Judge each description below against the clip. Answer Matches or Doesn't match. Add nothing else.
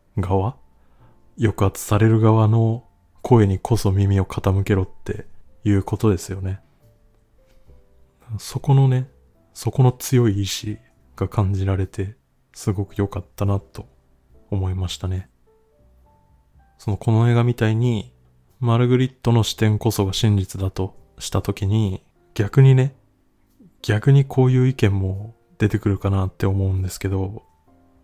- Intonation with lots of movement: Doesn't match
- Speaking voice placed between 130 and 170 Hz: Doesn't match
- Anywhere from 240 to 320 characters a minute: Matches